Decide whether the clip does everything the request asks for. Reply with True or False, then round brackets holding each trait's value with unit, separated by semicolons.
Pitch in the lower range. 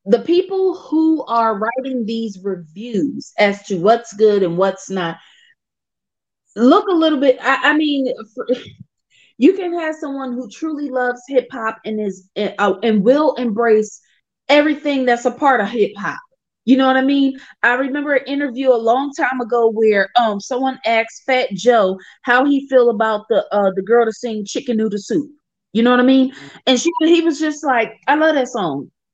False (250 Hz)